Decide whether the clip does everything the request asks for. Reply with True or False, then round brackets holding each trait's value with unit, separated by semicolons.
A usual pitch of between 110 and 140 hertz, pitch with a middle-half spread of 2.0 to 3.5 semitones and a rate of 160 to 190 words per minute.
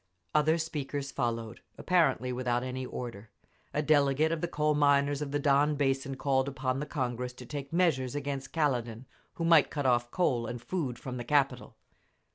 True (135 Hz; 2.9 semitones; 175 wpm)